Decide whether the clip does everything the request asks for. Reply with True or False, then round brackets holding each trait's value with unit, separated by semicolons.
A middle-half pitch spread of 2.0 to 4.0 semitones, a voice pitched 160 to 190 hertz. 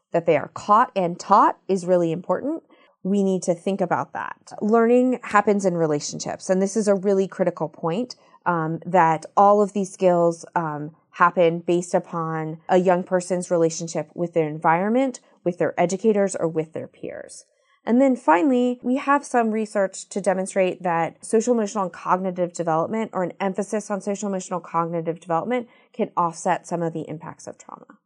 True (3.6 semitones; 185 Hz)